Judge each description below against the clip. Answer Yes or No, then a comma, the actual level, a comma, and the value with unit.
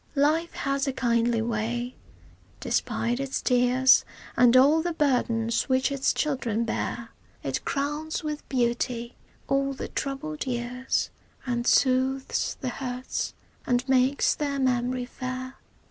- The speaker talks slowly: Yes, slow, 125 wpm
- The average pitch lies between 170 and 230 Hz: No, very high, 255 Hz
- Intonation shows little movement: Yes, narrow, 2.2 semitones